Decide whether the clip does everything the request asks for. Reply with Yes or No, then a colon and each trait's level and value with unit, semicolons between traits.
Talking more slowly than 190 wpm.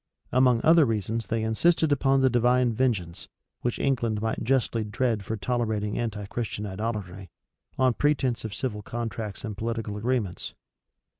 Yes: average, 145 wpm